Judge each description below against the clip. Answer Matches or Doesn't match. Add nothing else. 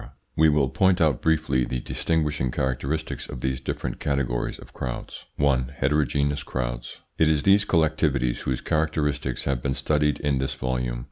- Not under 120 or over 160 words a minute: Matches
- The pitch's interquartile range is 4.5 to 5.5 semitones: Doesn't match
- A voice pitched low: Matches